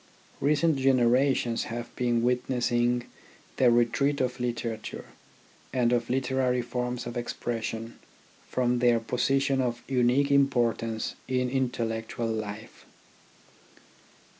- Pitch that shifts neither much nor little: No, narrow, 1.8 semitones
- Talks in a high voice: No, low, 125 Hz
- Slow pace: Yes, slow, 100 wpm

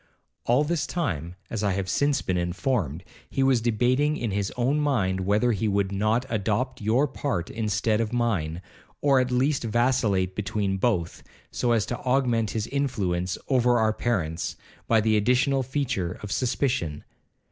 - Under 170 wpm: Yes, average, 160 wpm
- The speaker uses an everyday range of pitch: Yes, average, 4.8 semitones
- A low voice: Yes, low, 115 Hz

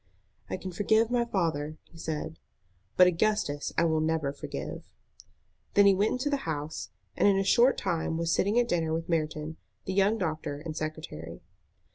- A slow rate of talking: No, average, 175 wpm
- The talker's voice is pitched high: No, medium, 165 Hz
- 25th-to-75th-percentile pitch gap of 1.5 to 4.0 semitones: No, average, 4.4 semitones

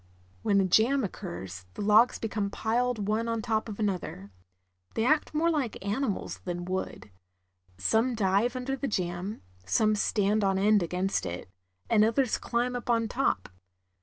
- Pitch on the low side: No, high, 215 Hz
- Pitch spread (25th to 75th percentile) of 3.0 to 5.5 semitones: Yes, average, 3.8 semitones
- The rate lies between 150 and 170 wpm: Yes, average, 160 wpm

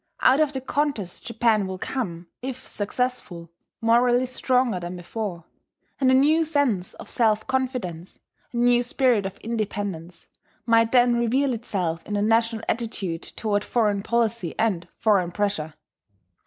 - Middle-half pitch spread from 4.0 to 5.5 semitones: Yes, average, 4.5 semitones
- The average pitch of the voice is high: Yes, high, 225 Hz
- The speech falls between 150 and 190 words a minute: No, average, 140 wpm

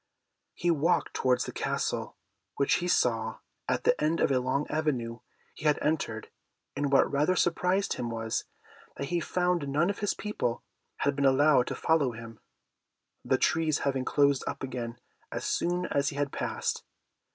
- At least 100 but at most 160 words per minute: No, average, 170 wpm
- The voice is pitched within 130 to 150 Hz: Yes, medium, 140 Hz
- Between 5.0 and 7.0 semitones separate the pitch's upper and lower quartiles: No, average, 4.4 semitones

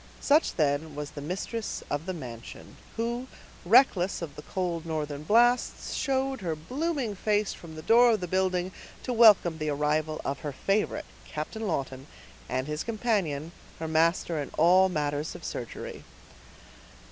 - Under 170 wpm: Yes, average, 150 wpm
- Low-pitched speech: No, medium, 170 Hz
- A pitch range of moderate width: No, wide, 6.5 semitones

